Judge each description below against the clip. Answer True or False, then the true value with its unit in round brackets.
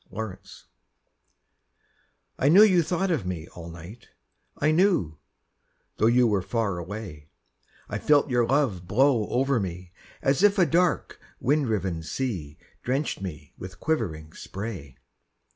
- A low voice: True (110 Hz)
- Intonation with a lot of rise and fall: True (8.4 semitones)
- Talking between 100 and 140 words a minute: True (135 wpm)